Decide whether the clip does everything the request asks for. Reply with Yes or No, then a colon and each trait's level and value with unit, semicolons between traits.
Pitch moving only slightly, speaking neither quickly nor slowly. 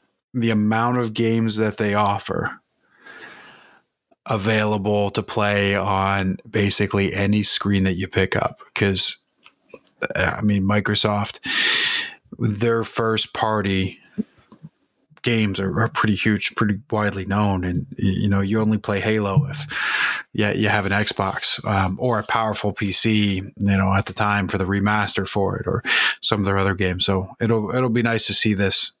Yes: narrow, 2.2 semitones; average, 150 wpm